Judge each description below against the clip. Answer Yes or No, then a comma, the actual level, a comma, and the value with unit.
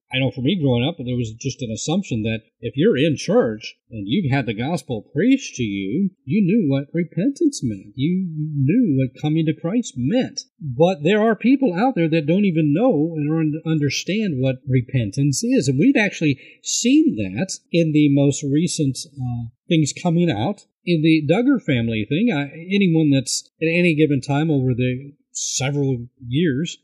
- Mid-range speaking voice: Yes, medium, 155 Hz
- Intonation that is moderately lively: No, wide, 6.1 semitones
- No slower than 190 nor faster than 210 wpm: No, average, 180 wpm